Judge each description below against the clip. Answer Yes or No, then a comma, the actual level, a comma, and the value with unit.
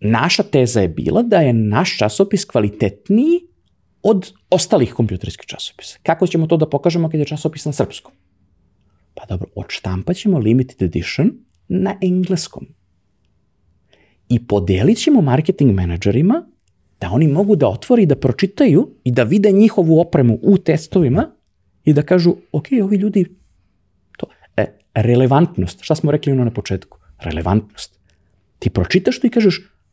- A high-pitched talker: No, low, 135 Hz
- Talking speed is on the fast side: No, average, 145 wpm